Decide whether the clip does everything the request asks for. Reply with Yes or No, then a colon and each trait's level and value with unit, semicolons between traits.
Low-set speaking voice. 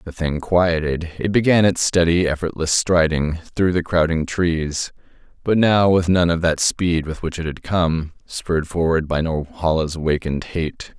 Yes: very low, 85 Hz